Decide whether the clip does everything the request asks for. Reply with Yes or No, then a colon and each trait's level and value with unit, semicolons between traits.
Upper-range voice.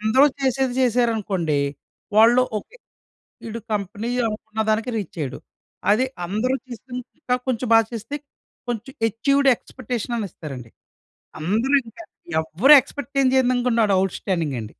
Yes: high, 230 Hz